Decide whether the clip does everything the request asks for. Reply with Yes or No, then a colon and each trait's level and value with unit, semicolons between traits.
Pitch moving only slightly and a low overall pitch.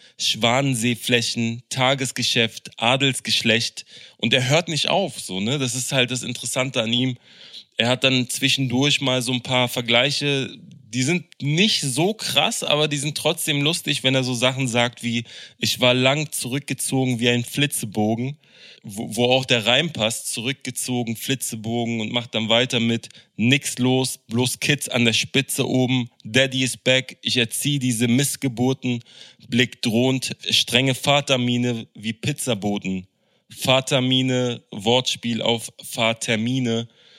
Yes: narrow, 2.3 semitones; low, 125 Hz